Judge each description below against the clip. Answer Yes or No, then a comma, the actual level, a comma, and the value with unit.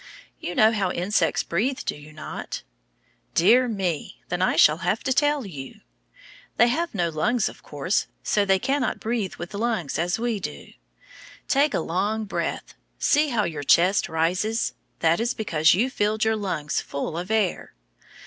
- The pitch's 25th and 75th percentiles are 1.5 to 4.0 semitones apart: No, average, 5.2 semitones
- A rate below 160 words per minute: No, average, 170 wpm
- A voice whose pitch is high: Yes, high, 200 Hz